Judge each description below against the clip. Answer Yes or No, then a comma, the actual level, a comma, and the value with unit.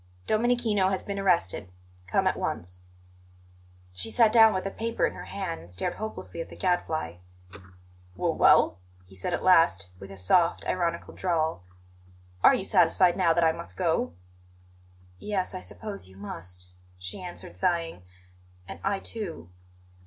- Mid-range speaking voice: Yes, medium, 170 Hz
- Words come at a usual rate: Yes, average, 155 wpm